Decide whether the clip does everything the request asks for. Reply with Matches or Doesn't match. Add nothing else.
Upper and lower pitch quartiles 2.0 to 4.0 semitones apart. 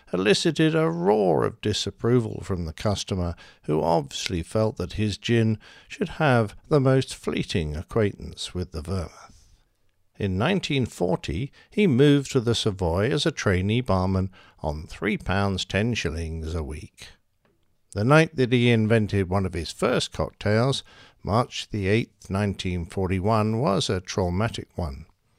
Doesn't match